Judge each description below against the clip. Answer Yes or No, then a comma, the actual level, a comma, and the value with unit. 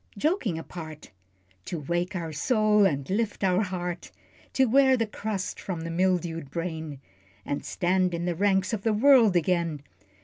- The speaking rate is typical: Yes, average, 160 wpm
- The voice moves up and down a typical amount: Yes, average, 4.0 semitones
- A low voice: No, medium, 180 Hz